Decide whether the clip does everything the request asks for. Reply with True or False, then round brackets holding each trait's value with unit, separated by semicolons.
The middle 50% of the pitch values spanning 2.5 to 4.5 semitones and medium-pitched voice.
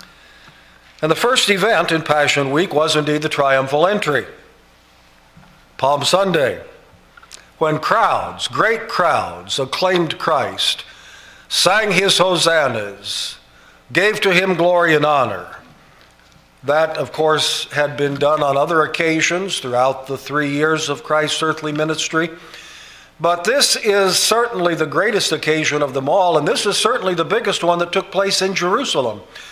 True (4.1 semitones; 160 Hz)